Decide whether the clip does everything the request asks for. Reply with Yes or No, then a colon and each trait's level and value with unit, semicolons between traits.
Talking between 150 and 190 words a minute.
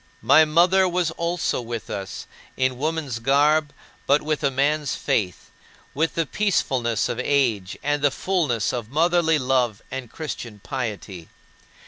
No: average, 140 wpm